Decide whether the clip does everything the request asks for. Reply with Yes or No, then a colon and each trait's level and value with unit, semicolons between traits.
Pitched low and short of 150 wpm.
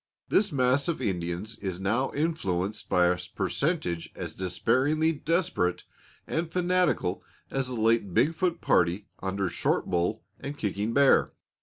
Yes: low, 115 Hz; average, 140 wpm